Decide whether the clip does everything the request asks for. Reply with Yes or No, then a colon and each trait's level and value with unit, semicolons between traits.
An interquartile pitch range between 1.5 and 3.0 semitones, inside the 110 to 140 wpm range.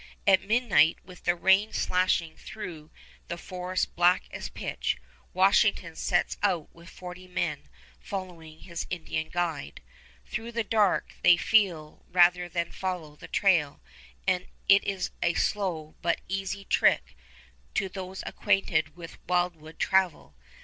Yes: narrow, 2.4 semitones; slow, 135 wpm